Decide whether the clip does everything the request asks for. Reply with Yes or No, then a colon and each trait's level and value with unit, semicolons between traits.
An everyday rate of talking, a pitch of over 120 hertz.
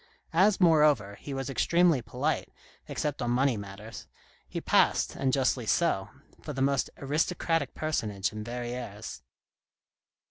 No: slow, 130 wpm; low, 135 Hz